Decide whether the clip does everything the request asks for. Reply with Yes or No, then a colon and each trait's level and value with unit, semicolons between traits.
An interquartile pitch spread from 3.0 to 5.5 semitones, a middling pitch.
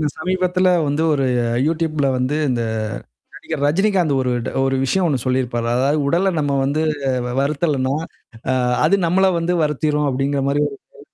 Yes: average, 4.0 semitones; medium, 150 Hz